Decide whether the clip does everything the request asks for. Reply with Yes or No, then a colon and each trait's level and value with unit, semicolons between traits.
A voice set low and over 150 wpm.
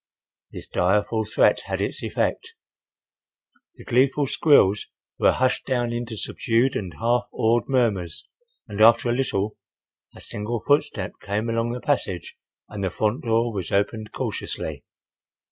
No: low, 115 Hz; average, 140 wpm